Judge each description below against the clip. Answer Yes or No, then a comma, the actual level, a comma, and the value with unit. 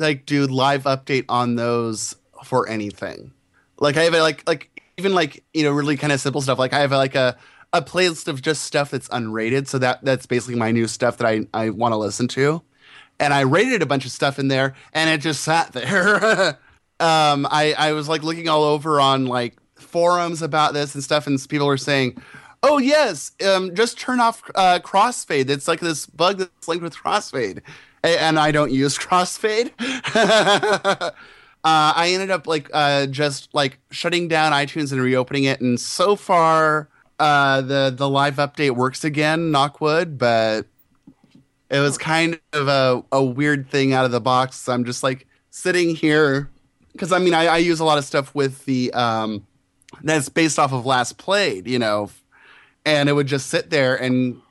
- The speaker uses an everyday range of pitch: Yes, average, 3.6 semitones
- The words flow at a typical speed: Yes, average, 195 wpm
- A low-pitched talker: No, medium, 145 Hz